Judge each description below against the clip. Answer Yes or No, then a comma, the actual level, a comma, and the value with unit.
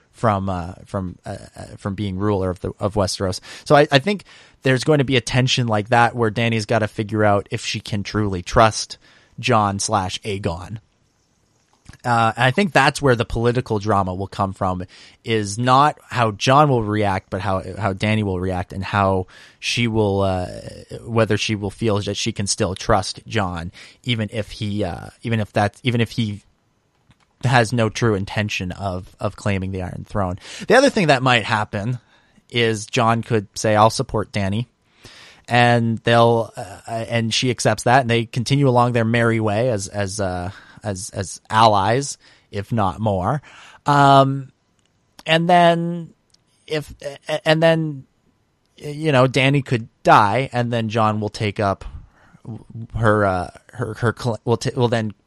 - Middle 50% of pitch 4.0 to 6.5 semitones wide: No, average, 3.4 semitones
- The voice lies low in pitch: Yes, low, 110 Hz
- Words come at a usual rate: Yes, average, 170 wpm